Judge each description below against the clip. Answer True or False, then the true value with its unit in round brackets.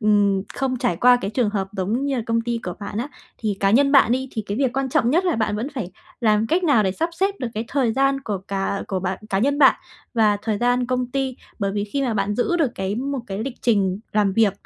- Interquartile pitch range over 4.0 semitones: True (4.7 semitones)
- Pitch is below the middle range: False (230 Hz)